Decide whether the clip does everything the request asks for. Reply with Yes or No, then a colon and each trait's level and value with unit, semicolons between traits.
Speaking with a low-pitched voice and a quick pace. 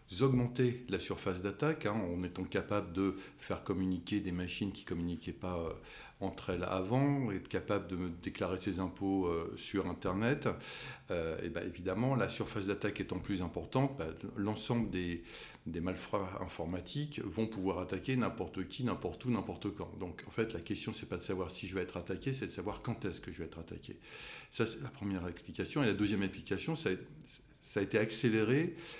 No: low, 100 Hz; average, 195 wpm